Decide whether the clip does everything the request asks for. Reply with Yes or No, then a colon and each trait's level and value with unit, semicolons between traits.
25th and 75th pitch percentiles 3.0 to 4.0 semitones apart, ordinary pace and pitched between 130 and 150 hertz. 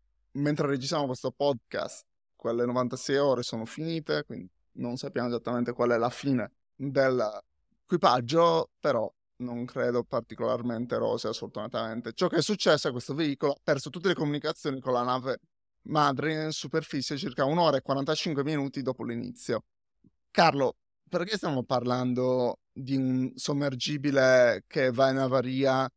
Yes: average, 3.3 semitones; average, 140 wpm; low, 135 Hz